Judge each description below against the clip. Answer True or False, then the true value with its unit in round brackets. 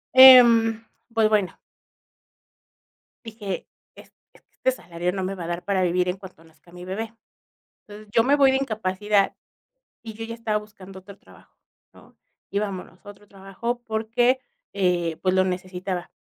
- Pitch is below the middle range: False (200 Hz)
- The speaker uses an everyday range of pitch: True (3.4 semitones)